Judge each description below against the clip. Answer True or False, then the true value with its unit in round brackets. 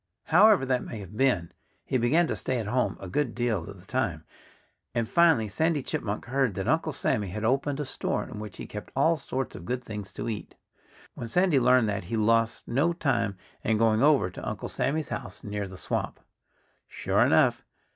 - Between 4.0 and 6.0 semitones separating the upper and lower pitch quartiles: True (4.6 semitones)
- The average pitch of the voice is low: True (120 Hz)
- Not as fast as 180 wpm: False (200 wpm)